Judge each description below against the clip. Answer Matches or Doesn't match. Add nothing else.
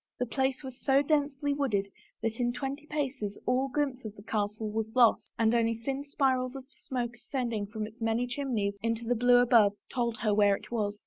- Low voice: Doesn't match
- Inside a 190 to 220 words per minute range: Matches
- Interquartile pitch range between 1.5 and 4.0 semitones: Matches